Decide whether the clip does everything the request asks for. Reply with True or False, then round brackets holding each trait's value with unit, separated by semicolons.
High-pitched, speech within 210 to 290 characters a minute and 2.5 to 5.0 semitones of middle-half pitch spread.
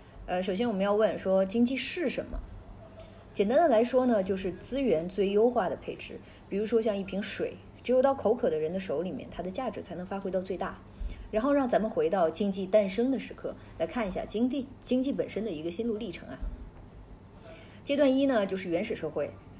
False (210 Hz; 305 characters per minute; 4.6 semitones)